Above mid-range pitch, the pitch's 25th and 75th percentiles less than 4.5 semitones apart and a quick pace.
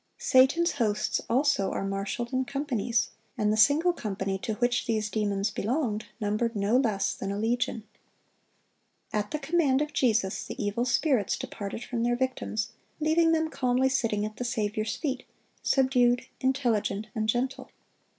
No: high, 235 Hz; average, 3.8 semitones; average, 150 wpm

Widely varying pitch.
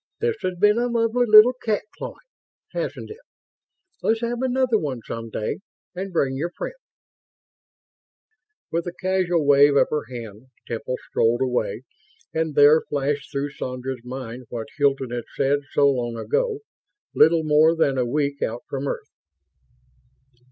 Yes: wide, 7.2 semitones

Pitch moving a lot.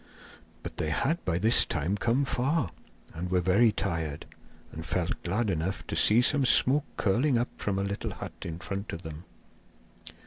Yes: wide, 5.9 semitones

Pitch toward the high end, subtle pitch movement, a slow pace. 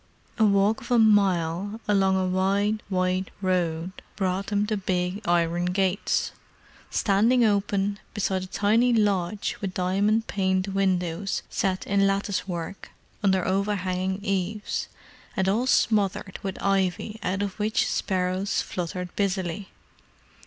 Yes: high, 195 Hz; narrow, 1.8 semitones; slow, 130 wpm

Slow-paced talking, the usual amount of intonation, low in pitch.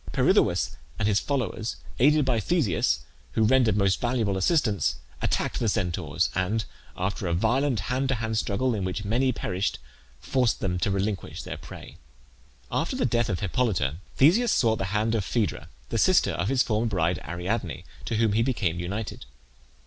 No: average, 170 wpm; average, 4.5 semitones; low, 110 Hz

